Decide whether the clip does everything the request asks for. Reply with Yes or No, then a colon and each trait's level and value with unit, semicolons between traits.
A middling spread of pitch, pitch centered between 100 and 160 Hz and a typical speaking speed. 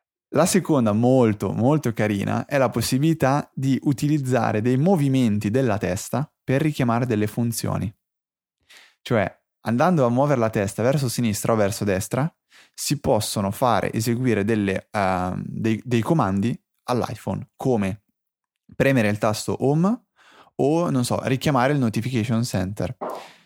Yes: average, 4.0 semitones; low, 120 Hz; average, 130 wpm